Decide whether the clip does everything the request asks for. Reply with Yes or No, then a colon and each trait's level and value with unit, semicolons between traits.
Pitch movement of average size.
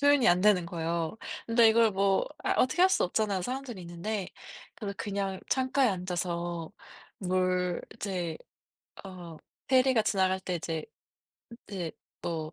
Yes: average, 4.2 semitones